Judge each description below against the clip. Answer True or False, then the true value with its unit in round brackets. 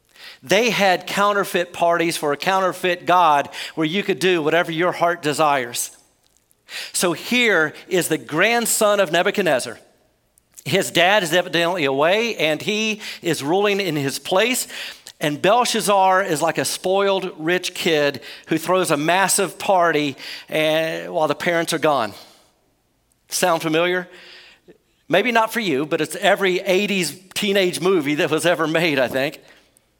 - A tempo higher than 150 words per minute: False (140 wpm)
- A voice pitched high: False (175 Hz)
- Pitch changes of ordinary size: True (3.5 semitones)